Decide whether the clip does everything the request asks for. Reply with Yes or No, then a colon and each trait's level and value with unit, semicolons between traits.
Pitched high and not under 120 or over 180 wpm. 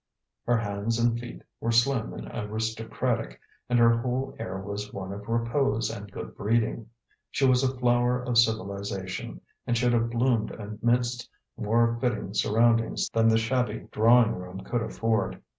No: low, 115 Hz; average, 155 wpm